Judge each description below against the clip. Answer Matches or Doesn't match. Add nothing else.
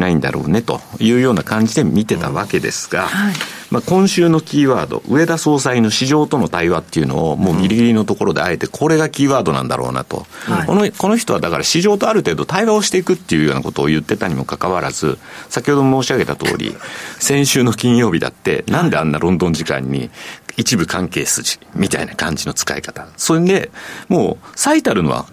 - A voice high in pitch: Doesn't match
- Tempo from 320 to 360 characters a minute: Doesn't match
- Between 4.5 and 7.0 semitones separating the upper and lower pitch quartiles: Doesn't match